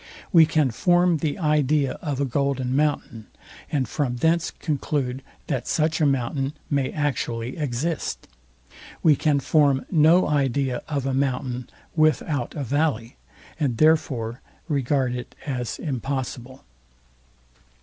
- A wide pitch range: No, average, 3.2 semitones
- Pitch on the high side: No, medium, 140 Hz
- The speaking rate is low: Yes, slow, 125 wpm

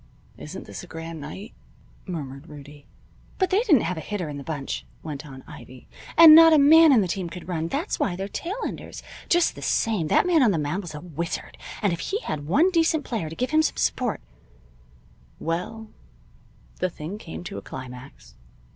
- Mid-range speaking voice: Yes, medium, 175 Hz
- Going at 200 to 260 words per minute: Yes, fast, 205 wpm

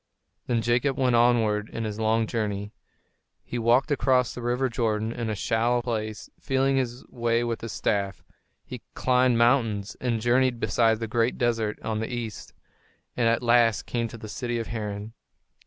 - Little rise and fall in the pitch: Yes, narrow, 1.9 semitones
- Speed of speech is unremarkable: Yes, average, 170 wpm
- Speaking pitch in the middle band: No, low, 115 Hz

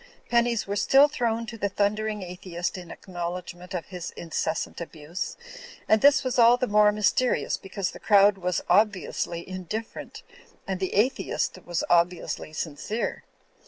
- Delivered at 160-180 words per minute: No, average, 150 wpm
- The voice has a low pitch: No, high, 195 Hz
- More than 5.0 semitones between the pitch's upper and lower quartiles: No, average, 3.9 semitones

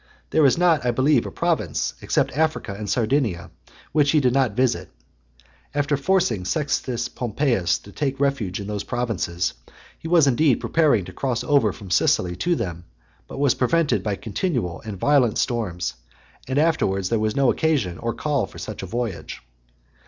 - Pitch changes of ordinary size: No, wide, 5.9 semitones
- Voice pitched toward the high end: No, low, 125 Hz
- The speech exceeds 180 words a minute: No, average, 170 wpm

